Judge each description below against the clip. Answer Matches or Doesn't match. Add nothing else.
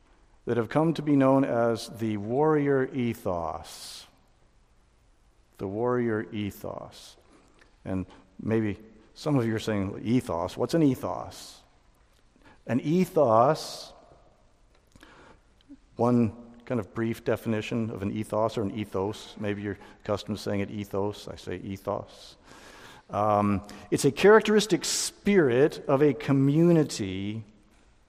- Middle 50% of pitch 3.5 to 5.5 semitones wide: Matches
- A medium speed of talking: Doesn't match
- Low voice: Matches